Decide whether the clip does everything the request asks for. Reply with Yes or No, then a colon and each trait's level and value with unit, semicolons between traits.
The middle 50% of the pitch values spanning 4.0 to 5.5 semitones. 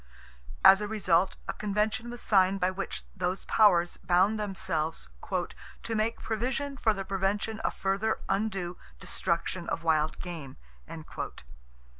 No: average, 3.2 semitones